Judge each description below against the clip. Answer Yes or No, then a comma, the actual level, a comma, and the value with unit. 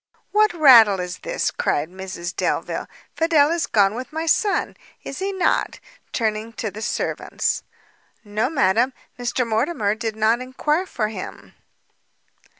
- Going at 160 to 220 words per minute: No, average, 140 wpm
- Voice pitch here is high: Yes, high, 235 Hz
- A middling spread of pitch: No, wide, 6.6 semitones